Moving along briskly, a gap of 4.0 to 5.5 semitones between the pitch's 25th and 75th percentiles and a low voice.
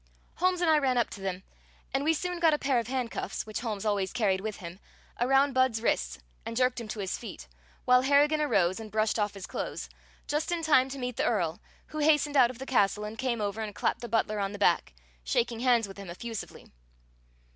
No: fast, 225 wpm; average, 4.7 semitones; high, 235 Hz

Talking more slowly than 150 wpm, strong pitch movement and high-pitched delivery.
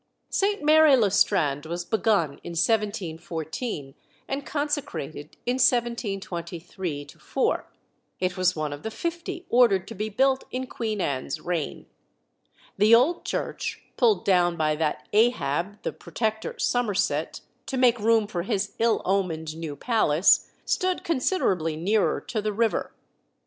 Yes: slow, 135 wpm; wide, 6.5 semitones; high, 205 Hz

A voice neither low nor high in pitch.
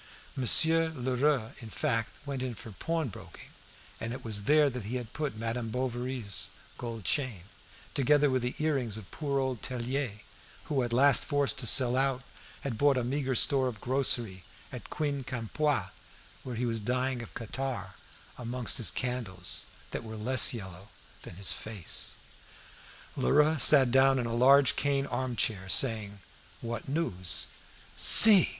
No: low, 125 Hz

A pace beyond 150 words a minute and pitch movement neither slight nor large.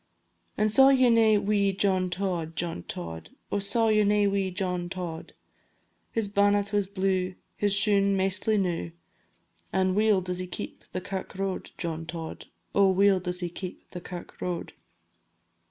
No: average, 160 wpm; narrow, 2.1 semitones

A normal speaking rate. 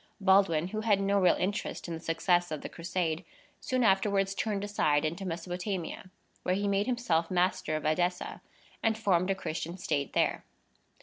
Yes: average, 170 wpm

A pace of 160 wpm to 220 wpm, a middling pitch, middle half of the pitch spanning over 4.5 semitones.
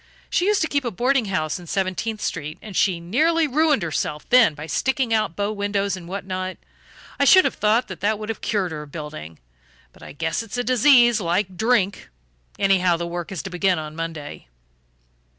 No: average, 200 wpm; high, 195 Hz; average, 5.3 semitones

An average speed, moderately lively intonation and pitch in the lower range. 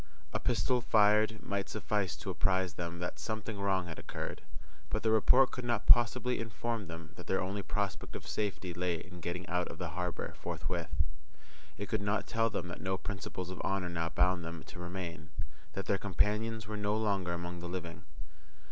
Yes: average, 185 wpm; average, 3.5 semitones; very low, 95 Hz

